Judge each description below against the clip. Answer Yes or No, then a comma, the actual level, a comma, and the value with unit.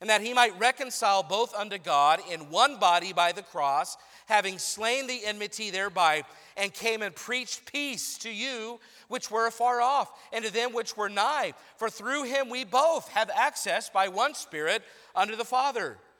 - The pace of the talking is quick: No, average, 180 wpm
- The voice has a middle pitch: No, high, 225 Hz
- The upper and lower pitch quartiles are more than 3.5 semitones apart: Yes, average, 4.0 semitones